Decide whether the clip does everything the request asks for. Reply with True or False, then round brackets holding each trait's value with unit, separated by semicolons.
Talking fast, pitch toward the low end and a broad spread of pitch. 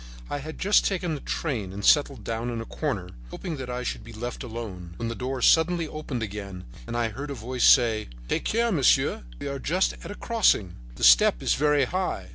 True (220 wpm; 125 Hz; 5.7 semitones)